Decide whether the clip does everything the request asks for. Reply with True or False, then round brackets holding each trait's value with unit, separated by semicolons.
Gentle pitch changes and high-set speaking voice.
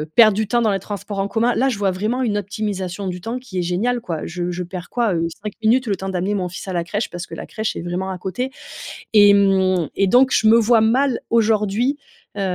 False (3.6 semitones; 205 Hz)